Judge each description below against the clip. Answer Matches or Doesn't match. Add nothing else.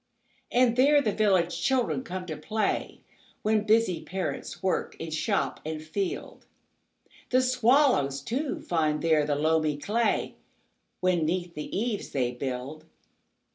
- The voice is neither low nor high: Matches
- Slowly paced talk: Matches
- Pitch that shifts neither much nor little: Doesn't match